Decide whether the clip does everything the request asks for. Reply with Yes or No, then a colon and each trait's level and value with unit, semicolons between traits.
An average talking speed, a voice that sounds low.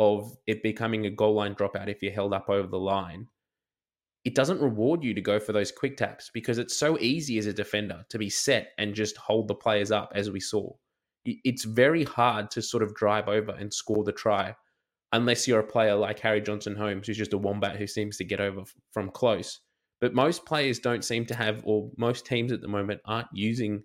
No: fast, 225 wpm; low, 105 Hz